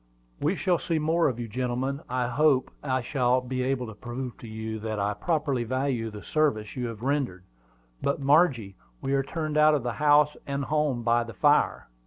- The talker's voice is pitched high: No, low, 130 Hz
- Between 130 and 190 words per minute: No, average, 200 wpm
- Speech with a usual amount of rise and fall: Yes, average, 4.0 semitones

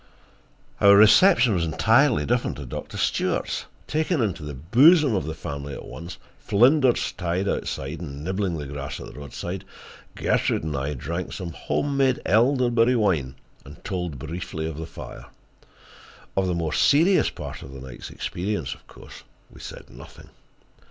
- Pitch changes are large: Yes, wide, 8.1 semitones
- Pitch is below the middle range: Yes, very low, 90 Hz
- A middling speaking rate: Yes, average, 160 wpm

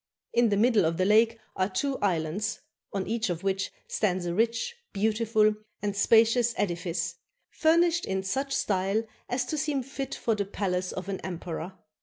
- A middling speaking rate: Yes, average, 170 wpm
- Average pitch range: Yes, average, 4.0 semitones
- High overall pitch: Yes, high, 205 Hz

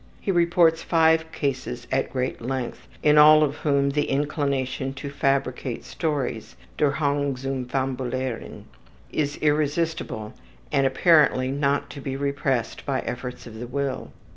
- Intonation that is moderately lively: No, narrow, 2.3 semitones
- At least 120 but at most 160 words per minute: Yes, average, 140 wpm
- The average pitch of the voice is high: No, medium, 140 Hz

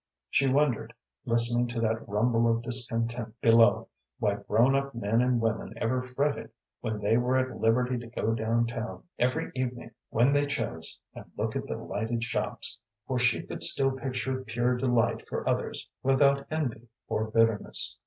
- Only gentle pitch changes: Yes, narrow, 2.1 semitones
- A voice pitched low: Yes, low, 120 Hz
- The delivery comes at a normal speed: Yes, average, 165 wpm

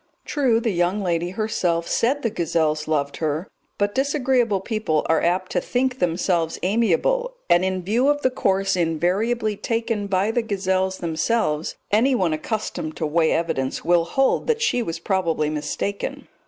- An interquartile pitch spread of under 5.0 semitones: No, wide, 5.5 semitones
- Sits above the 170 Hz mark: Yes, high, 190 Hz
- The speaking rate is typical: Yes, average, 155 wpm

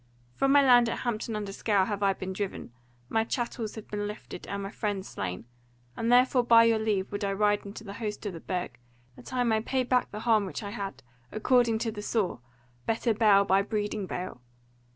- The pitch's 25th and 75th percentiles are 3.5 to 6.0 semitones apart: No, narrow, 2.5 semitones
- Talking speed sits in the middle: No, fast, 215 wpm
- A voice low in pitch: No, high, 210 Hz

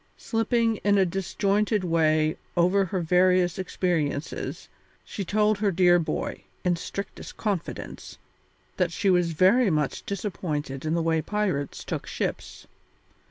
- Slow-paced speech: Yes, slow, 130 wpm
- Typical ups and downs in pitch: Yes, average, 3.4 semitones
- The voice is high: No, medium, 180 Hz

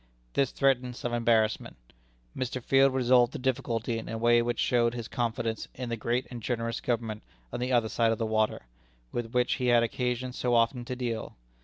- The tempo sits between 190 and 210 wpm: Yes, average, 195 wpm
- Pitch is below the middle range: Yes, low, 120 Hz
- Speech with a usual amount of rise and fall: No, narrow, 1.5 semitones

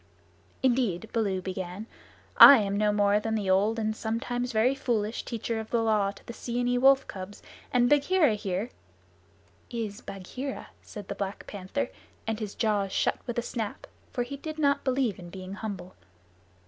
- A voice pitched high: Yes, high, 220 Hz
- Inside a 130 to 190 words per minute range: Yes, average, 175 wpm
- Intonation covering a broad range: No, average, 3.5 semitones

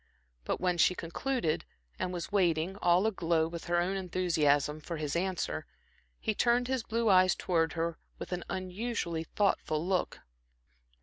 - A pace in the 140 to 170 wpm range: Yes, average, 150 wpm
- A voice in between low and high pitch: Yes, medium, 180 Hz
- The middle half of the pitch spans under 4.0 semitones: Yes, average, 2.8 semitones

